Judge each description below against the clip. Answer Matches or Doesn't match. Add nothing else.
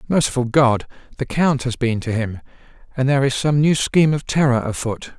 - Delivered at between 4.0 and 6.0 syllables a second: Matches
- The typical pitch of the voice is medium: Doesn't match